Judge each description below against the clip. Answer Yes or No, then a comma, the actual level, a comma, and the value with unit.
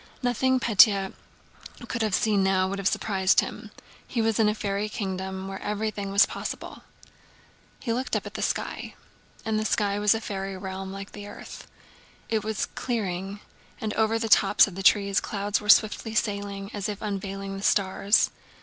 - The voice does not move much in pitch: Yes, narrow, 1.8 semitones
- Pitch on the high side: Yes, high, 205 Hz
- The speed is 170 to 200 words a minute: Yes, average, 175 wpm